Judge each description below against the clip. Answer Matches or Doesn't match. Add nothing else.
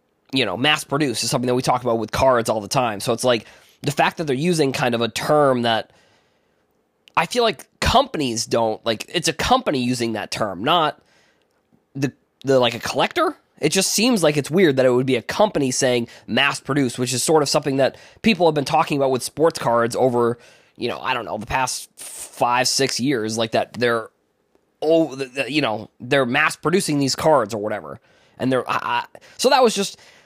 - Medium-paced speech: Doesn't match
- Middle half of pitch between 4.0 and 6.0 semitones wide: Matches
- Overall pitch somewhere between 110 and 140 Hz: Matches